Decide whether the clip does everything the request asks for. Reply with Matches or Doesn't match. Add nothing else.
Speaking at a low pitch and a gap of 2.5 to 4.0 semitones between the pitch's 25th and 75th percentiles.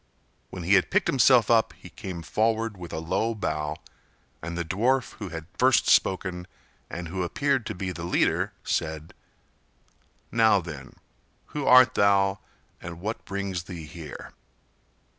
Doesn't match